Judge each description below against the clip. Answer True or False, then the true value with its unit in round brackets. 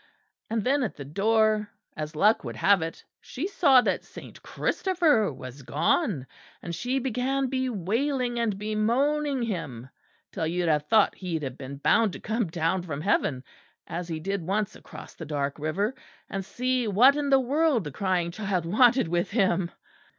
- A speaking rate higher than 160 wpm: True (170 wpm)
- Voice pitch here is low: False (200 Hz)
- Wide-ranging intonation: True (7.2 semitones)